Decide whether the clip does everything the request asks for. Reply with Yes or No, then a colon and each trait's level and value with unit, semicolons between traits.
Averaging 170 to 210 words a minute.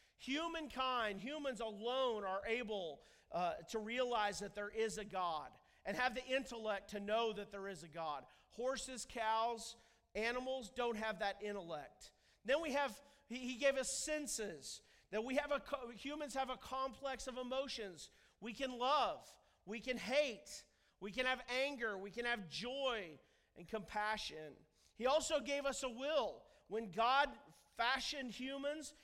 No: average, 150 wpm